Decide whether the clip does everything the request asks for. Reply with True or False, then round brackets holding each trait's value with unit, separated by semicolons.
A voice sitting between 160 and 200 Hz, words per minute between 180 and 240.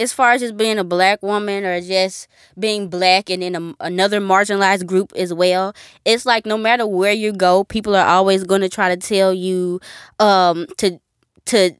True (190 Hz; 200 wpm)